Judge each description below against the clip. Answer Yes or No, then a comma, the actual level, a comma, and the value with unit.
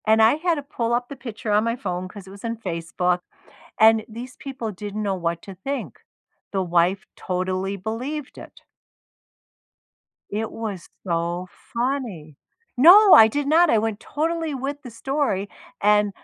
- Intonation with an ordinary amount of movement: No, wide, 6.0 semitones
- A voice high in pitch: Yes, high, 220 Hz